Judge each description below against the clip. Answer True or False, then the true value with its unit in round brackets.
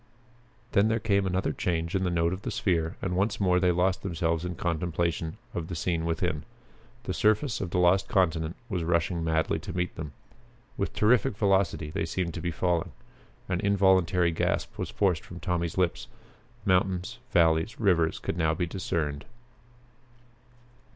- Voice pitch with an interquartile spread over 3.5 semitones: False (2.4 semitones)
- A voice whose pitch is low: True (90 Hz)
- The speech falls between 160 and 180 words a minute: True (165 wpm)